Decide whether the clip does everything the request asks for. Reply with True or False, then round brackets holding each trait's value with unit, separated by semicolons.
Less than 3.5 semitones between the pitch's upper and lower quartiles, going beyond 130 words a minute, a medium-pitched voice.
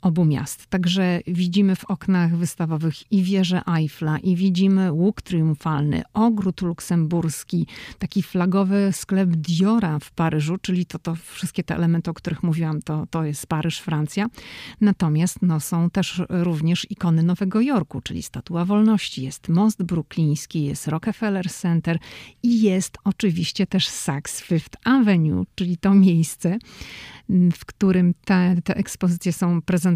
True (2.8 semitones; 140 wpm; 175 Hz)